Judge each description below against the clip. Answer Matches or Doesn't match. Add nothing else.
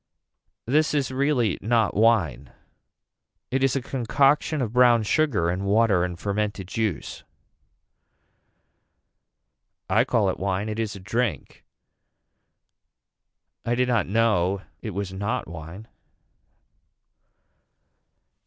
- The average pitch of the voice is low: Matches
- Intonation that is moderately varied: Matches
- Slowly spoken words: Matches